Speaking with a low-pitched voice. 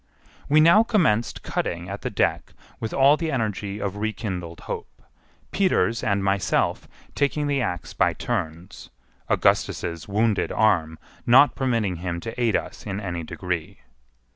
Yes: low, 105 Hz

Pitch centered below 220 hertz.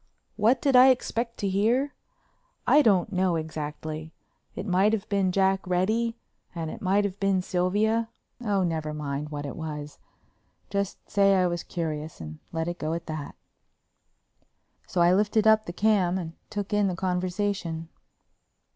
Yes: medium, 185 Hz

